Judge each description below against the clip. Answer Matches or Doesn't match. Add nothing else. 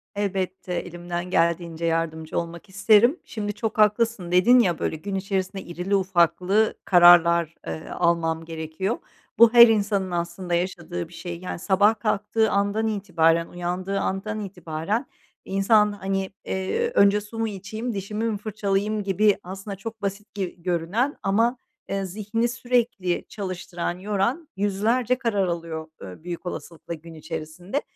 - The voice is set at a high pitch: Matches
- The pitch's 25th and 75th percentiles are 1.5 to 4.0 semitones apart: Matches